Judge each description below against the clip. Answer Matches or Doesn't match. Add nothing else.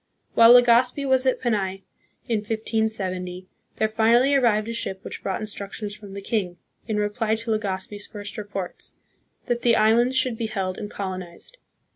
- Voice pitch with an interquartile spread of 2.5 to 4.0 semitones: Matches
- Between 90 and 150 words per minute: Doesn't match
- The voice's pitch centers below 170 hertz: Doesn't match